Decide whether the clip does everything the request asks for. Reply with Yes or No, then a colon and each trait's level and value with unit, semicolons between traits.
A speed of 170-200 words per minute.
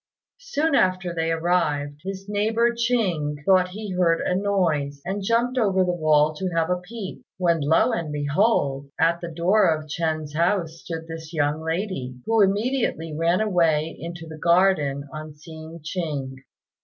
No: average, 160 wpm